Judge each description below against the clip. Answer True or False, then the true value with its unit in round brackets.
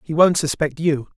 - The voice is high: False (155 Hz)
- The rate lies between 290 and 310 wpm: False (205 wpm)